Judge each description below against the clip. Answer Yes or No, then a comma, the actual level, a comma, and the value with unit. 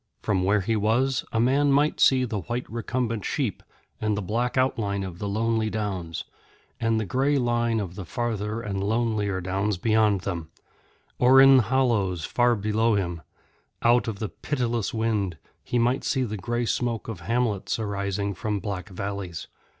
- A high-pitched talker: No, low, 110 Hz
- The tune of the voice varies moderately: Yes, average, 3.2 semitones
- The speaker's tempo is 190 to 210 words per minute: No, average, 165 wpm